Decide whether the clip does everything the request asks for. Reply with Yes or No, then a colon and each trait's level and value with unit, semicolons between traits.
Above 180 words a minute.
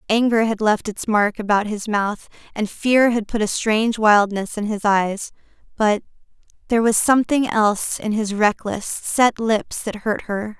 No: average, 165 wpm